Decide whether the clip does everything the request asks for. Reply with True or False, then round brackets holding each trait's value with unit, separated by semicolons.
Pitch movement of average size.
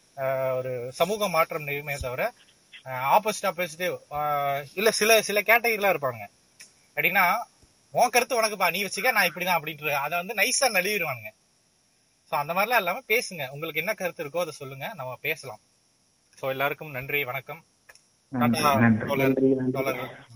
False (6.6 semitones)